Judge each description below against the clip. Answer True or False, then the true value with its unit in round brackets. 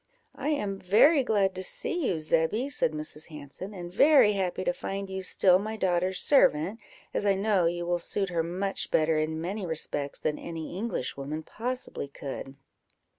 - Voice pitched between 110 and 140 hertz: False (185 Hz)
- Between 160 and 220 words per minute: True (175 wpm)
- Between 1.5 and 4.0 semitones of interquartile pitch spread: False (4.4 semitones)